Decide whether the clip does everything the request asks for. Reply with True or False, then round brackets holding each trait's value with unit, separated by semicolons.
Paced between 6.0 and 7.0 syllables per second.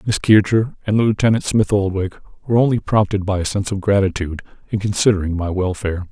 True (6.1 syllables/s)